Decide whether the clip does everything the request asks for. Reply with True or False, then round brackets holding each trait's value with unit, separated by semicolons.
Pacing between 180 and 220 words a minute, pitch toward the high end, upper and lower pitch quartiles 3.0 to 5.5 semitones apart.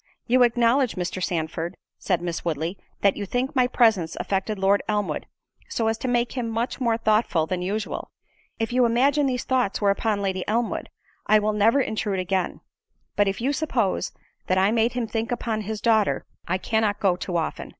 True (190 wpm; 215 Hz; 3.8 semitones)